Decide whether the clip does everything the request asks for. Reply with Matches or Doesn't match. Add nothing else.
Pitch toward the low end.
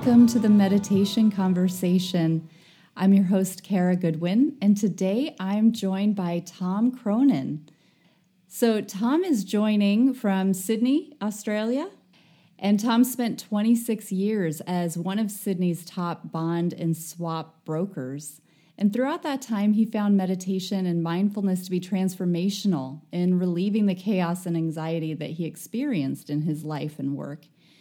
Doesn't match